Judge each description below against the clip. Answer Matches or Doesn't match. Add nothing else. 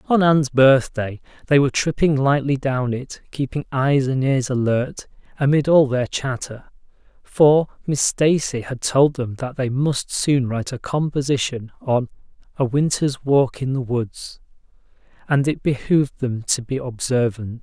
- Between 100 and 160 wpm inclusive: Matches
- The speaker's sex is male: Matches